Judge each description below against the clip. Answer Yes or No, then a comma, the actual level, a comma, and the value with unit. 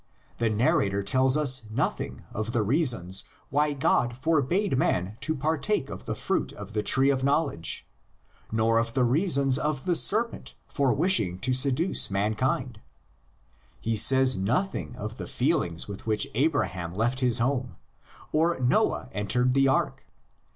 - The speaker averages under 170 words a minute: Yes, average, 150 wpm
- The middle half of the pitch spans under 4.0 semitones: No, average, 4.9 semitones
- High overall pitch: No, low, 130 Hz